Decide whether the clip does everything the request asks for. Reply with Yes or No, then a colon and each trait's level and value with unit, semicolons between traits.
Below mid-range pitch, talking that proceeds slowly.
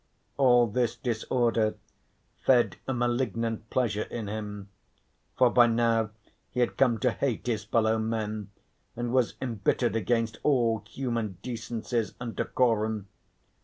Yes: low, 115 Hz; slow, 130 wpm